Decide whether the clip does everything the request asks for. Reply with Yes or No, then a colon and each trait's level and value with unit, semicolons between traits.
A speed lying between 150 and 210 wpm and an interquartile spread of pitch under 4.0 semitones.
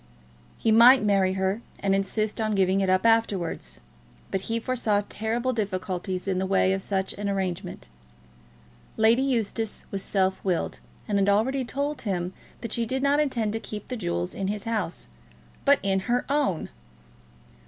Yes: average, 165 wpm; average, 3.3 semitones